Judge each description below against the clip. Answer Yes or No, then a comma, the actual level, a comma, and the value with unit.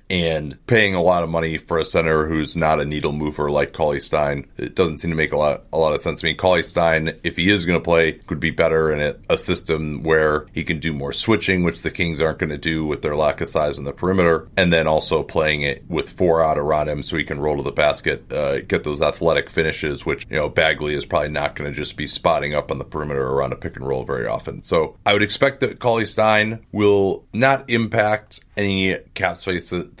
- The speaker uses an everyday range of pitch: Yes, average, 3.7 semitones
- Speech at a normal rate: No, fast, 250 wpm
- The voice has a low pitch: Yes, very low, 80 Hz